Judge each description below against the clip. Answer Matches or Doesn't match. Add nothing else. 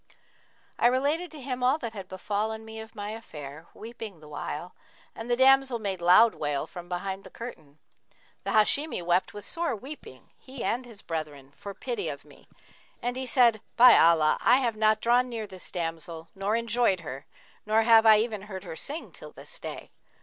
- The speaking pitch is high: Matches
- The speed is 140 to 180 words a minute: Doesn't match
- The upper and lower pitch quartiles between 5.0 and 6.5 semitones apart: Matches